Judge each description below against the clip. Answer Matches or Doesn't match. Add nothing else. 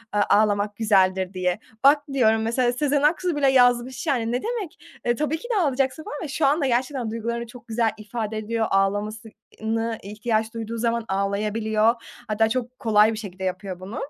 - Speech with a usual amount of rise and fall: Matches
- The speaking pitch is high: Matches